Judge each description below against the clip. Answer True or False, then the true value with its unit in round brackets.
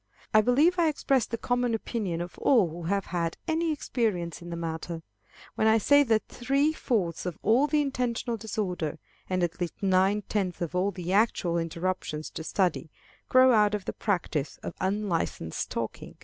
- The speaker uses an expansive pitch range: True (5.9 semitones)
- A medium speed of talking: True (175 wpm)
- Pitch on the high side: True (200 Hz)